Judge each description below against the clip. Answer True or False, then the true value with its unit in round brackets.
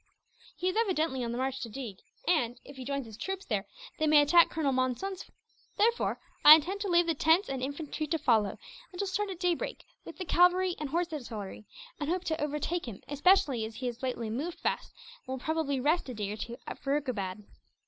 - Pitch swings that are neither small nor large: False (5.8 semitones)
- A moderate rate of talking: False (220 wpm)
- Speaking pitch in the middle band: False (290 Hz)